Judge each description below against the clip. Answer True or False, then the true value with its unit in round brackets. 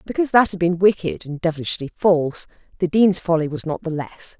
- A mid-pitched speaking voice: True (175 Hz)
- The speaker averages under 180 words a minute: False (205 wpm)